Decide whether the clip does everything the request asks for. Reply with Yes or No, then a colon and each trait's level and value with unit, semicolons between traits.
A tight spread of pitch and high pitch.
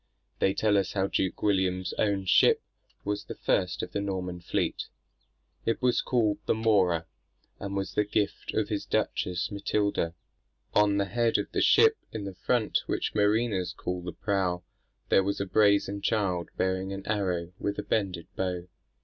No: narrow, 2.2 semitones; low, 100 Hz